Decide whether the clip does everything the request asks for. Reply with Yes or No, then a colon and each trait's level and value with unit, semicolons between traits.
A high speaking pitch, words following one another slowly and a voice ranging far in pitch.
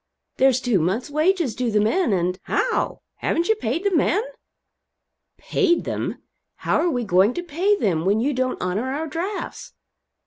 No: very high, 260 Hz; average, 175 wpm; wide, 8.6 semitones